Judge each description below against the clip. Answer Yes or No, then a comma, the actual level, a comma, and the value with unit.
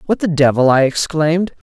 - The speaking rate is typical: Yes, average, 175 wpm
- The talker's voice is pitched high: No, medium, 155 Hz